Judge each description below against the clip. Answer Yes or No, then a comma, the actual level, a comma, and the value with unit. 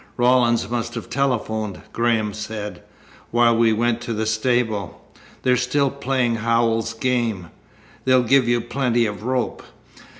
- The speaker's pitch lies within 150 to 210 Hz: No, low, 120 Hz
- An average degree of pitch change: No, narrow, 2.3 semitones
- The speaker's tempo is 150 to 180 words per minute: No, slow, 135 wpm